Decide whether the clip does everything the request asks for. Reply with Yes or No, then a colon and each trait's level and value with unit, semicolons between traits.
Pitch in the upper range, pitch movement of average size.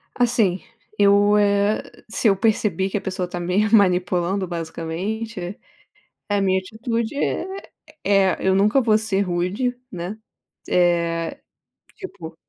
Yes: high, 195 Hz; average, 3.2 semitones